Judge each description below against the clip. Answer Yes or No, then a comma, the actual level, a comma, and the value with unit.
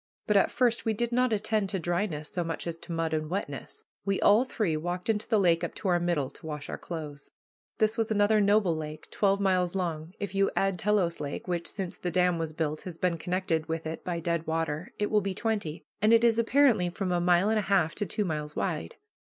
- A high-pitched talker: No, medium, 180 Hz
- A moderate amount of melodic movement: Yes, average, 4.2 semitones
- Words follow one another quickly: Yes, fast, 235 wpm